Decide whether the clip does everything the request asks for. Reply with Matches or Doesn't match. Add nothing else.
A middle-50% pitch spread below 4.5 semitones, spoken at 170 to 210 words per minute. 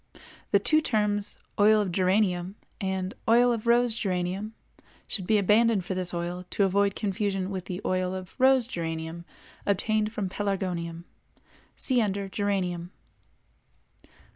Doesn't match